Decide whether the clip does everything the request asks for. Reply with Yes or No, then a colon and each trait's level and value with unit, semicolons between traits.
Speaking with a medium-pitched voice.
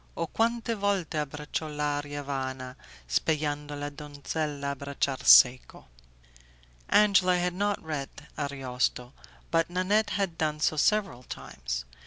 Yes: medium, 150 Hz